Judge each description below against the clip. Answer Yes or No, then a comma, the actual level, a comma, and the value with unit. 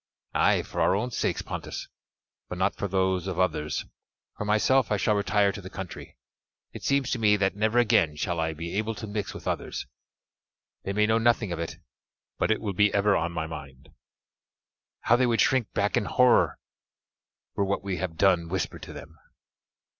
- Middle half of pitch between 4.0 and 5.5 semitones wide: No, average, 3.4 semitones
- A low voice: Yes, low, 100 Hz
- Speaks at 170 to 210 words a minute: Yes, average, 190 wpm